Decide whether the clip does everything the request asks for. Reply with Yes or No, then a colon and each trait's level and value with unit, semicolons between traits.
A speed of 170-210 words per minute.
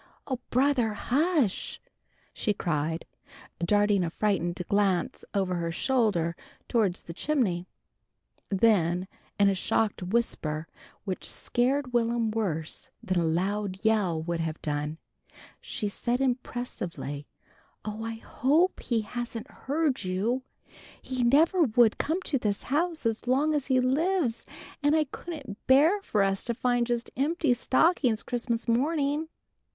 No: slow, 135 wpm